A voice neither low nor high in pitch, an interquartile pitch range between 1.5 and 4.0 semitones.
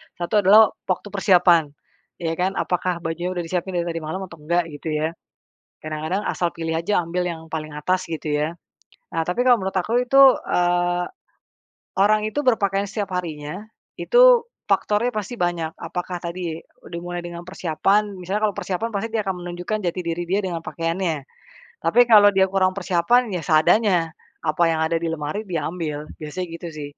Yes: medium, 175 Hz; average, 3.1 semitones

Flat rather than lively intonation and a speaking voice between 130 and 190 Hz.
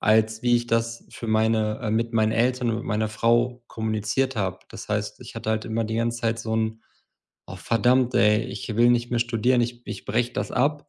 No: narrow, 1.6 semitones; low, 115 Hz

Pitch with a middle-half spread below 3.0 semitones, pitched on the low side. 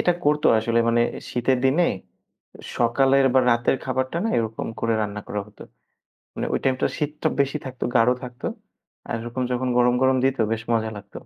Yes: narrow, 2.4 semitones; low, 125 Hz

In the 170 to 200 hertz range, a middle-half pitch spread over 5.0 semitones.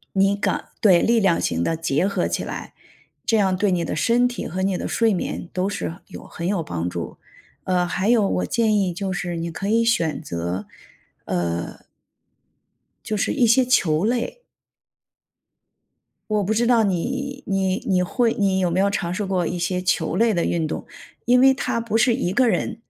No: high, 195 Hz; average, 4.7 semitones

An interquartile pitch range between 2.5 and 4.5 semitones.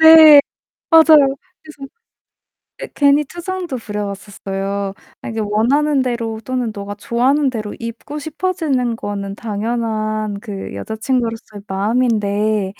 No: average, 5.3 semitones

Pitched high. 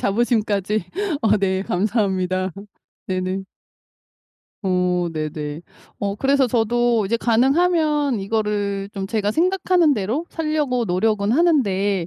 Yes: high, 210 Hz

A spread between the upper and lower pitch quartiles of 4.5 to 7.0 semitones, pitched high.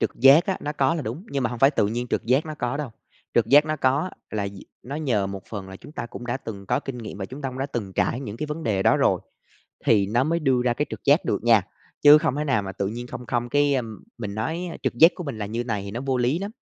No: average, 4.8 semitones; low, 125 Hz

